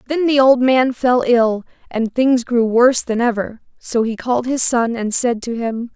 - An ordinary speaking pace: No, fast, 210 wpm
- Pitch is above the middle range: Yes, high, 240 Hz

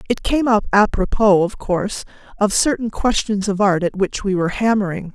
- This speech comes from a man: No, female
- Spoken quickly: No, average, 185 wpm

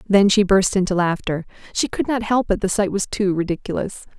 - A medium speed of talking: No, fast, 215 wpm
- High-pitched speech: Yes, high, 195 Hz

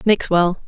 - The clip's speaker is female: Yes, female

